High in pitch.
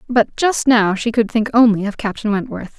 Yes: high, 220 Hz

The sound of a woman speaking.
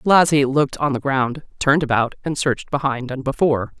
Yes: female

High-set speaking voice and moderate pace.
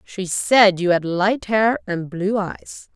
Yes: high, 195 Hz; average, 185 wpm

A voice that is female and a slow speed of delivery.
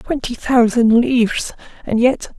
Yes: female; slow, 125 wpm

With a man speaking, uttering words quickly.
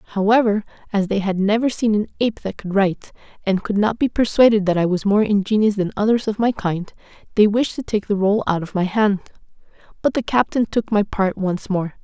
No: female; fast, 220 wpm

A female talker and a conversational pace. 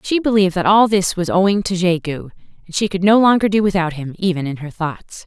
No: female; fast, 250 wpm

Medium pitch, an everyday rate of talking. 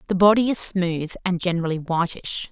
Yes: medium, 180 Hz; average, 165 wpm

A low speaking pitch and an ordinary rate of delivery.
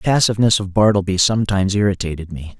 Yes: low, 100 Hz; average, 160 wpm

